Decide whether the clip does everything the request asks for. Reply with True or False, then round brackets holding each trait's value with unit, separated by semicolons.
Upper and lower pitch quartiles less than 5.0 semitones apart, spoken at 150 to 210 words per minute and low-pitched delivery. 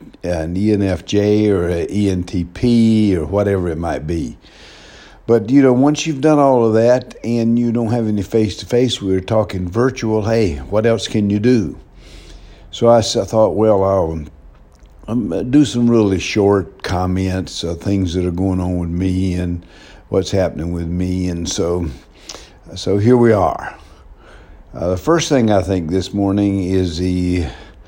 True (4.2 semitones; 160 wpm; 100 Hz)